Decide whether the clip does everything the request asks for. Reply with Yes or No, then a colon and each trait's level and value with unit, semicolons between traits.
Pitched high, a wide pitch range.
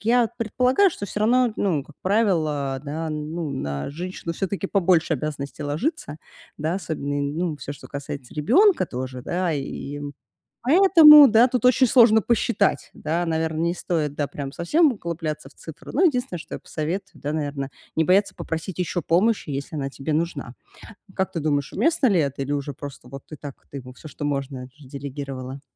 No: medium, 160 Hz; wide, 6.0 semitones